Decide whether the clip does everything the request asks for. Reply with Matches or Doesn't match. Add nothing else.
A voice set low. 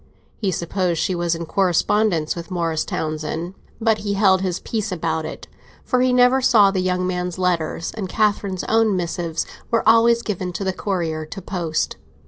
Doesn't match